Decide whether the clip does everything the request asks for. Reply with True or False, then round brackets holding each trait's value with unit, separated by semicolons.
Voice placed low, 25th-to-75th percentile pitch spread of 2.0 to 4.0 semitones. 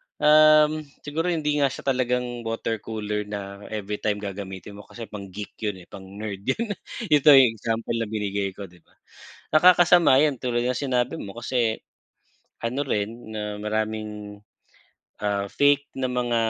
False (115 Hz; 4.5 semitones)